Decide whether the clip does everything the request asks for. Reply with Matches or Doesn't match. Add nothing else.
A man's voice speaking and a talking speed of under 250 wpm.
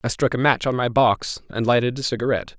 Doesn't match